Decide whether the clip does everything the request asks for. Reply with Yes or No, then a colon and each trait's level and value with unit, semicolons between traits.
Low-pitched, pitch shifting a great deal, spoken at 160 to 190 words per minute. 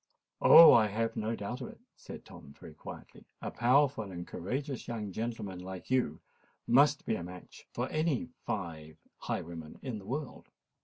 Yes: low, 110 Hz; wide, 6.0 semitones; average, 165 wpm